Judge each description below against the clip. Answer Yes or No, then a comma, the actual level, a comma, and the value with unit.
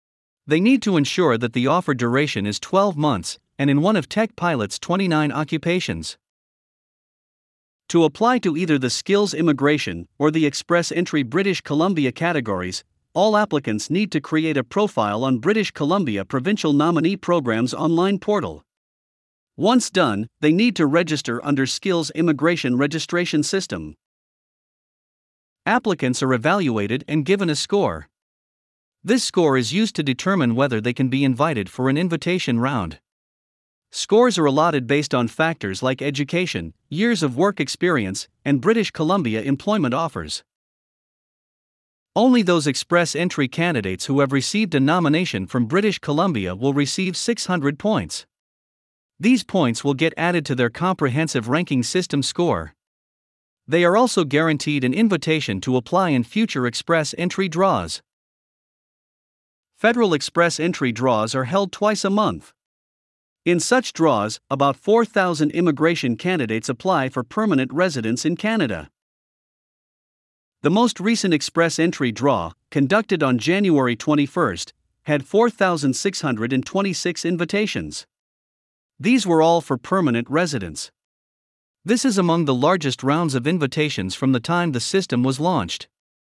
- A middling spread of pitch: No, wide, 5.8 semitones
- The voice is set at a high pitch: No, medium, 155 Hz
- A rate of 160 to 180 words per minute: No, slow, 135 wpm